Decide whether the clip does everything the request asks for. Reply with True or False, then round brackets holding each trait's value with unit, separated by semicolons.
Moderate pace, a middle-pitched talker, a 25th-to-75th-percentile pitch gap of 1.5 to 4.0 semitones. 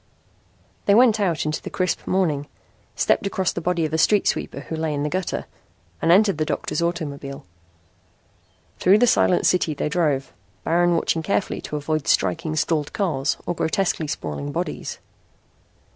True (160 wpm; 165 Hz; 3.4 semitones)